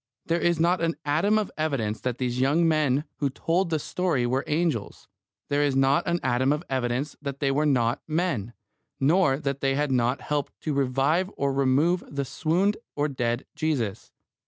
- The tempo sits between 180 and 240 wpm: Yes, average, 185 wpm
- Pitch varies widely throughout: No, average, 3.7 semitones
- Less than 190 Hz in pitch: Yes, medium, 140 Hz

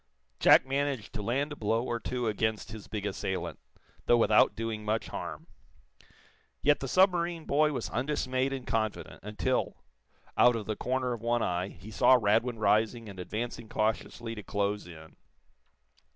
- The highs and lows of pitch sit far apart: No, average, 3.3 semitones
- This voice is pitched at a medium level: No, low, 115 Hz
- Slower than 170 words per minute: Yes, average, 160 wpm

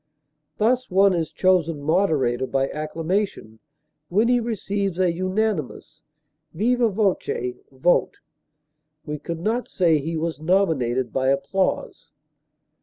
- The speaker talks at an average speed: No, slow, 110 wpm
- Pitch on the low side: No, medium, 175 Hz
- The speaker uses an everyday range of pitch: Yes, average, 5.0 semitones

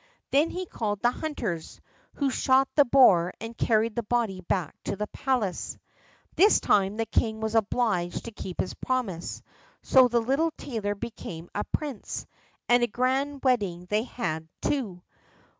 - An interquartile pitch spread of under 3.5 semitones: No, average, 4.8 semitones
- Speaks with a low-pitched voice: No, high, 225 Hz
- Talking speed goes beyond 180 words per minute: No, average, 160 wpm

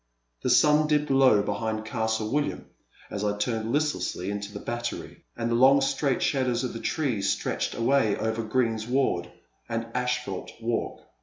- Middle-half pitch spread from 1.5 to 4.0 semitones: Yes, average, 3.5 semitones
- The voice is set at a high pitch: No, low, 115 Hz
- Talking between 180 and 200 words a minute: No, average, 155 wpm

